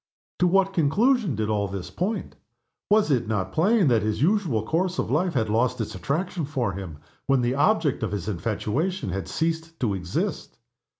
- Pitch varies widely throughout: Yes, wide, 8.9 semitones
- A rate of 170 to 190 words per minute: Yes, average, 180 wpm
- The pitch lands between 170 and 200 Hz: No, medium, 140 Hz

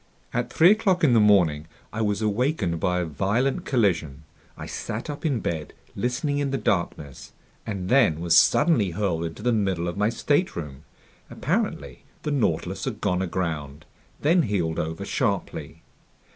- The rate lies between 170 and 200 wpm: No, average, 160 wpm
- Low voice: Yes, low, 100 Hz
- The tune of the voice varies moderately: No, wide, 7.3 semitones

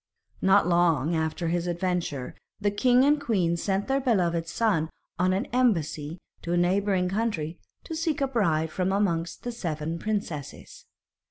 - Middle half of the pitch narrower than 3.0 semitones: No, average, 4.4 semitones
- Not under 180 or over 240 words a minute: No, average, 155 wpm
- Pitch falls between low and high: Yes, medium, 180 Hz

